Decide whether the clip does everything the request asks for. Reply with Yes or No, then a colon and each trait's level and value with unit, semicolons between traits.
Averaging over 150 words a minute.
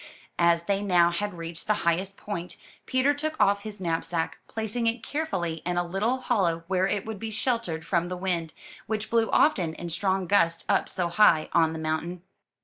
Yes: average, 190 wpm